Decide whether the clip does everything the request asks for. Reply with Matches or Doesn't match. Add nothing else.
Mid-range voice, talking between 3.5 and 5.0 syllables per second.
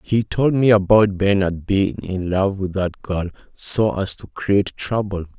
Doesn't match